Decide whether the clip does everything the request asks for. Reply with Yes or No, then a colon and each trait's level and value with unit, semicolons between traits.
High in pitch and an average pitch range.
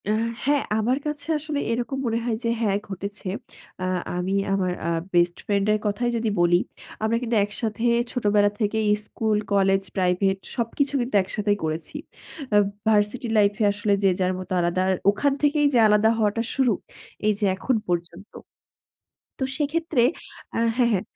Yes: high, 210 Hz; average, 3.7 semitones